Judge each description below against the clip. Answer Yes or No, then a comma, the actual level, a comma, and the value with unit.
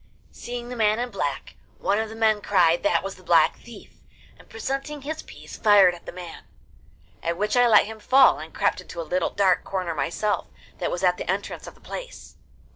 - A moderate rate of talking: No, fast, 210 wpm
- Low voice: No, high, 205 Hz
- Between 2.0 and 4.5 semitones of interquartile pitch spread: No, average, 4.9 semitones